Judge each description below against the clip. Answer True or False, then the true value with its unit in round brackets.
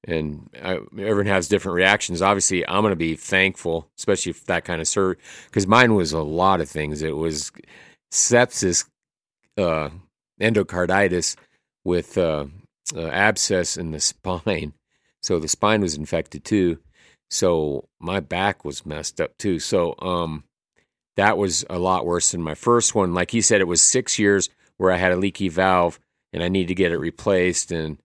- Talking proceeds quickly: False (175 wpm)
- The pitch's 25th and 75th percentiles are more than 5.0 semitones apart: False (3.2 semitones)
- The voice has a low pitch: True (90 Hz)